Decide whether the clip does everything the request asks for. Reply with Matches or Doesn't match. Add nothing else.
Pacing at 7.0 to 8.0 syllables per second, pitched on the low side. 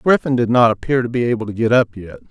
Matches